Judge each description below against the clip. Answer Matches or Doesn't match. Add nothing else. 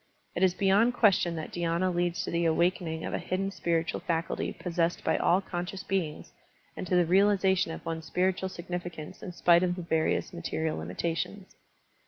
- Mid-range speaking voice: Matches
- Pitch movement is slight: Matches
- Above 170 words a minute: Matches